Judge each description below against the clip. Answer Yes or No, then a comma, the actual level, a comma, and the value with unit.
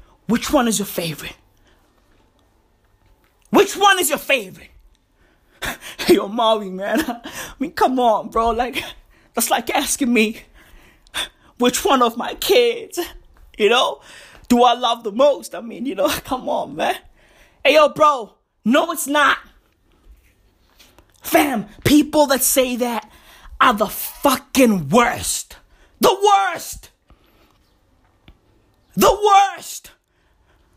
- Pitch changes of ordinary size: No, wide, 6.2 semitones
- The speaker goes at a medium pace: No, slow, 120 wpm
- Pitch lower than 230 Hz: No, very high, 255 Hz